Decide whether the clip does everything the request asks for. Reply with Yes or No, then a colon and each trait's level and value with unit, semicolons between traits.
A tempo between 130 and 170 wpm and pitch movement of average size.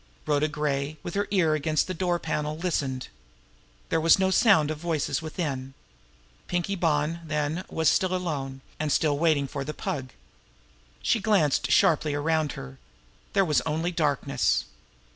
Yes: average, 155 wpm; average, 3.0 semitones